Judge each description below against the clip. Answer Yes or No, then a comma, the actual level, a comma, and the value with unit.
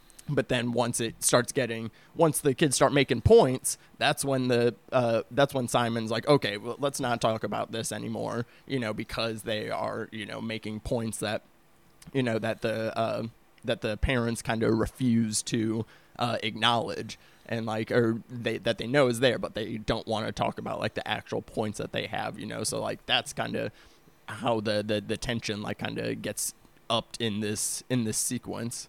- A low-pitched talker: Yes, low, 115 Hz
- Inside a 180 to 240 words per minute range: Yes, average, 200 wpm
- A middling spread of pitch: Yes, average, 3.0 semitones